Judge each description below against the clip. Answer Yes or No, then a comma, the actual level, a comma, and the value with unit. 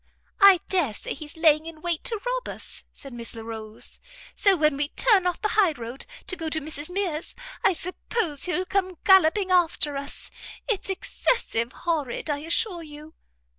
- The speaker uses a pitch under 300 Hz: No, very high, 325 Hz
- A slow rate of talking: No, average, 170 wpm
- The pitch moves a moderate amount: Yes, average, 4.3 semitones